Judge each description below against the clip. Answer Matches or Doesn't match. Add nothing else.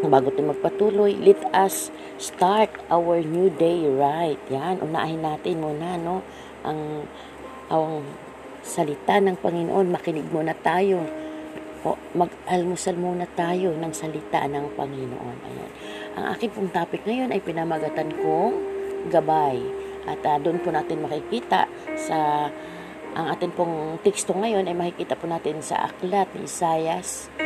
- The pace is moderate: Matches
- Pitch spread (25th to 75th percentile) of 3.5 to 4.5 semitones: Matches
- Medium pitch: Matches